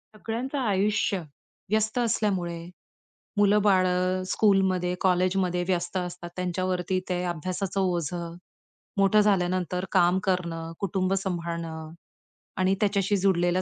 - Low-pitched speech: No, medium, 185 Hz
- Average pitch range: No, narrow, 1.9 semitones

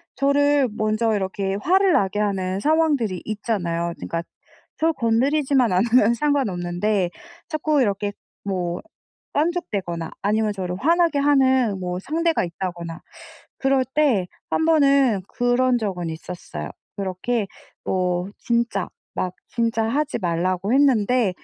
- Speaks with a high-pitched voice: Yes, high, 220 Hz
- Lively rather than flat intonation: Yes, wide, 6.9 semitones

